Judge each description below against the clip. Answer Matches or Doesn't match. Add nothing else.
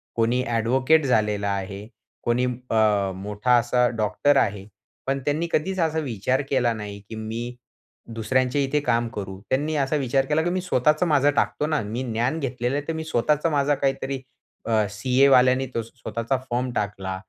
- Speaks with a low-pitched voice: Matches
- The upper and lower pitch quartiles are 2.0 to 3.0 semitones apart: Doesn't match